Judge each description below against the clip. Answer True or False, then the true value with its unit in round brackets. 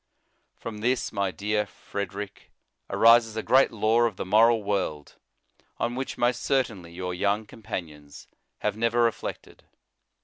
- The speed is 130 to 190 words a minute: True (140 wpm)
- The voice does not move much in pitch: False (3.2 semitones)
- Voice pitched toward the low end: True (105 Hz)